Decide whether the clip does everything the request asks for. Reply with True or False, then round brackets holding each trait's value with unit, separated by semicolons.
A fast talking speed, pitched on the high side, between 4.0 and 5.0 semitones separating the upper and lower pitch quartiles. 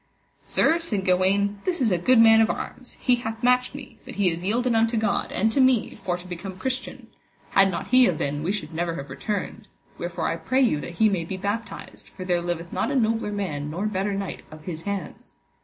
True (225 wpm; 200 Hz; 4.5 semitones)